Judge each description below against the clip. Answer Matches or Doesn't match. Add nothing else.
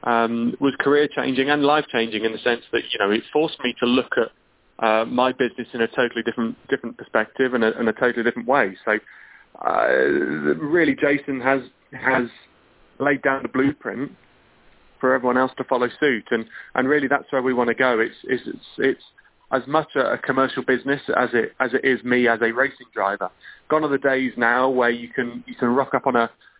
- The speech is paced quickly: Matches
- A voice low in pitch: Matches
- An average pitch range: Doesn't match